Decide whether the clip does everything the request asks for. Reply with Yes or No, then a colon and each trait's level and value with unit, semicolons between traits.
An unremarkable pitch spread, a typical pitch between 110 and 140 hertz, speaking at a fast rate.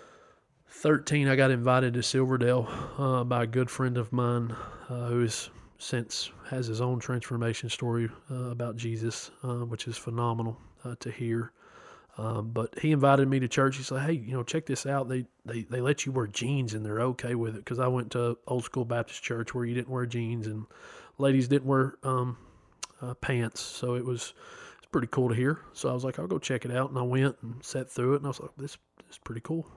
No: narrow, 2.1 semitones; low, 125 Hz; fast, 225 wpm